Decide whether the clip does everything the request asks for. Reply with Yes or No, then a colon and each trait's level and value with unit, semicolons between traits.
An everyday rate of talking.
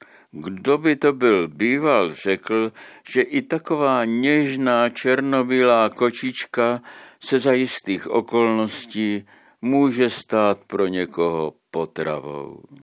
No: slow, 100 wpm